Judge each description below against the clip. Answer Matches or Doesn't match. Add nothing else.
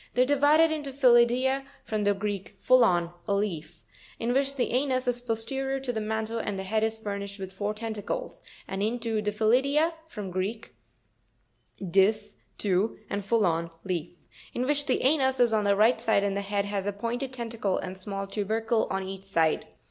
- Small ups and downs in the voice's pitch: Doesn't match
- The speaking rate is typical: Matches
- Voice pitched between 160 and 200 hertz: Doesn't match